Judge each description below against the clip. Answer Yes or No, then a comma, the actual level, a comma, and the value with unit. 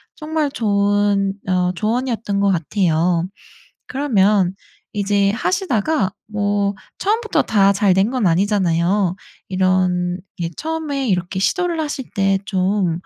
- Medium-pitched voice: No, high, 200 Hz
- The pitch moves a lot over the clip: No, average, 4.1 semitones